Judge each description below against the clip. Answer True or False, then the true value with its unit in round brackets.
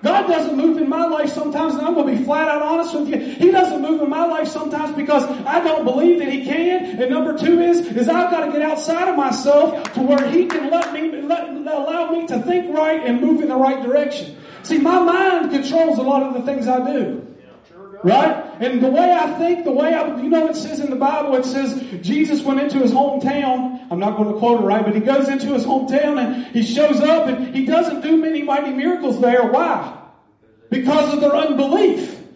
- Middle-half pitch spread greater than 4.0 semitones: False (3.2 semitones)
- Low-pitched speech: False (295 Hz)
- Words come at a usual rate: False (230 wpm)